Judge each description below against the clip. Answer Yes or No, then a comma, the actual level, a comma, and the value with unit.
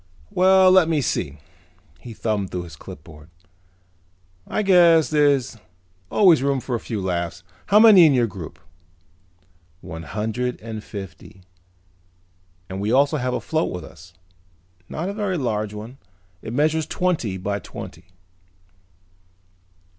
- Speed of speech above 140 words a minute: No, slow, 135 wpm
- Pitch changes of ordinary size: No, wide, 8.7 semitones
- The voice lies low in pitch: Yes, low, 120 Hz